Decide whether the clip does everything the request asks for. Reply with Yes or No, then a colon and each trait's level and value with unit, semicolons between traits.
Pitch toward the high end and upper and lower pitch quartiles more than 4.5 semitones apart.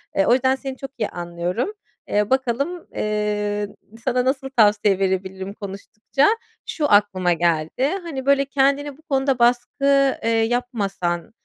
Yes: high, 235 Hz; average, 5.2 semitones